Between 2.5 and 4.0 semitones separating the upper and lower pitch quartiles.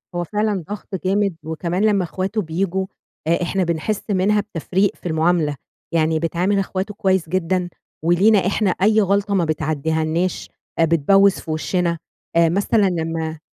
Yes: average, 3.2 semitones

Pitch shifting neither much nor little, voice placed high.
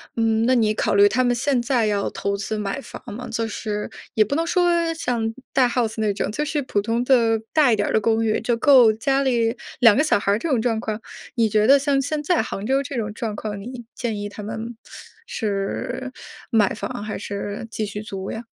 Yes: average, 3.4 semitones; high, 225 Hz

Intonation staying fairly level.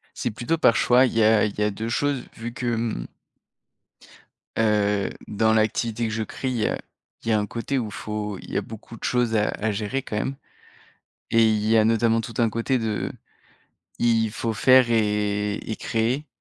Yes: narrow, 1.9 semitones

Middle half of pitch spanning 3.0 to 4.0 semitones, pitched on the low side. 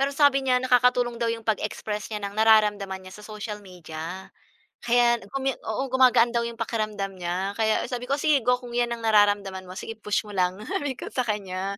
No: average, 3.5 semitones; high, 220 Hz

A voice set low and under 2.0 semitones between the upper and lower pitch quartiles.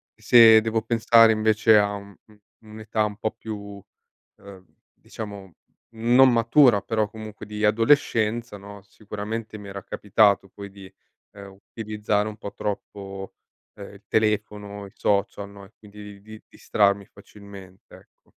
Yes: low, 105 Hz; narrow, 1.6 semitones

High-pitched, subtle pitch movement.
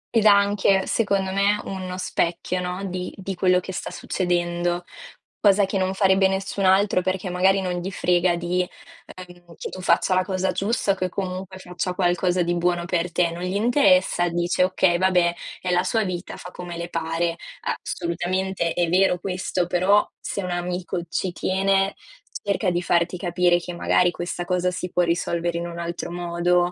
No: medium, 180 Hz; narrow, 1.5 semitones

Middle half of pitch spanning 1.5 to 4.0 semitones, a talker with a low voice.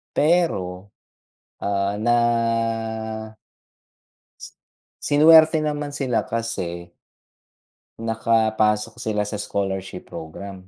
No: average, 5.3 semitones; low, 110 Hz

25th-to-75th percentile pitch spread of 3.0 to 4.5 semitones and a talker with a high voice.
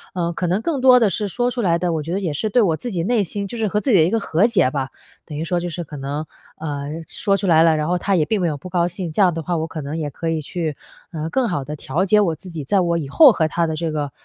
No: average, 4.1 semitones; medium, 170 Hz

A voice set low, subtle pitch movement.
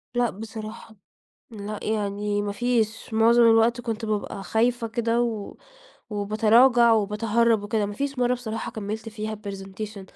No: high, 220 Hz; narrow, 2.1 semitones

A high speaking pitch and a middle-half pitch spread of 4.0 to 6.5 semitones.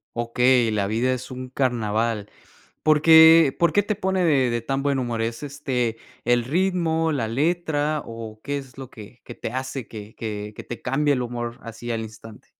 No: low, 125 Hz; average, 4.3 semitones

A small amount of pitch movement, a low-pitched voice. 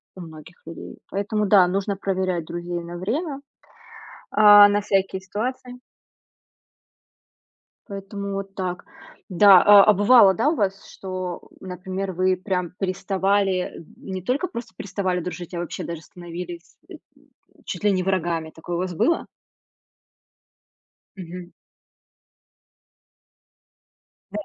No: narrow, 2.2 semitones; high, 190 Hz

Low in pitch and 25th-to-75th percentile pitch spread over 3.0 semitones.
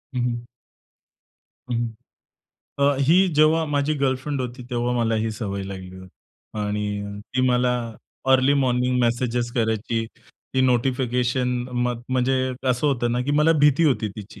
No: low, 125 Hz; average, 2.7 semitones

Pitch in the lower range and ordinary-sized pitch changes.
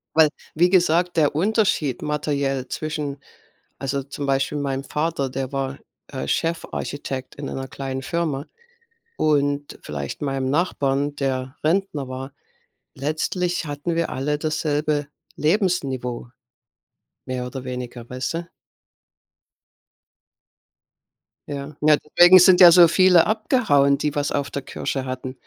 No: medium, 145 Hz; average, 3.2 semitones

